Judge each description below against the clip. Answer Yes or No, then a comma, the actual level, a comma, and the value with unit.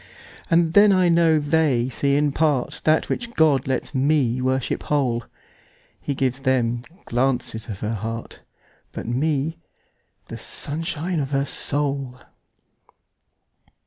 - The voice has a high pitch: No, medium, 140 Hz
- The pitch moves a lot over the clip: No, average, 3.7 semitones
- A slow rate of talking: Yes, slow, 115 wpm